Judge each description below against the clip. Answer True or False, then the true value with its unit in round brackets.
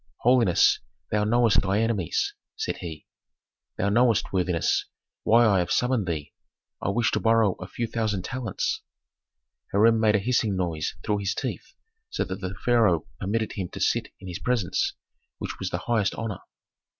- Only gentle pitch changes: False (3.6 semitones)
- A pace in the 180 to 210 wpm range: False (165 wpm)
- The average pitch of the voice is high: False (105 Hz)